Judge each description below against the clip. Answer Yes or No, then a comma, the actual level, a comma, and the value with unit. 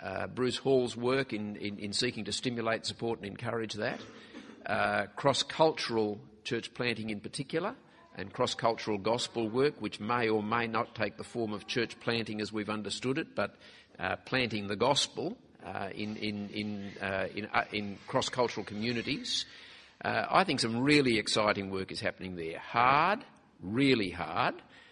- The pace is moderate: Yes, average, 170 wpm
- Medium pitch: No, low, 110 Hz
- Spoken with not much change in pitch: Yes, narrow, 2.3 semitones